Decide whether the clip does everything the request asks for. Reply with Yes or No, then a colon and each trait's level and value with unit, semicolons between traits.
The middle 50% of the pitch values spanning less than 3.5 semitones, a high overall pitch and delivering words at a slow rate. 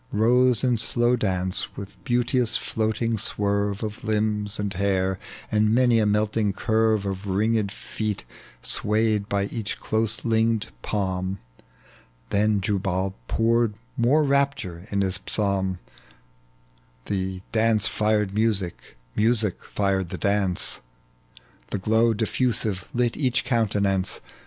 No: narrow, 2.5 semitones; low, 105 Hz; slow, 120 wpm